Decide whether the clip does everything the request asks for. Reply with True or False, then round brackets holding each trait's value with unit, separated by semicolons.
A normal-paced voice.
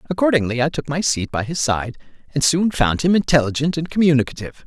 True (195 wpm)